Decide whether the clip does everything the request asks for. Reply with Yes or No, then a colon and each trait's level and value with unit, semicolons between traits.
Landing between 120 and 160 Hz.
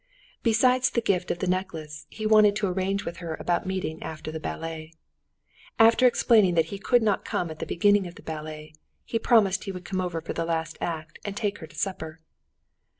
No: medium, 180 Hz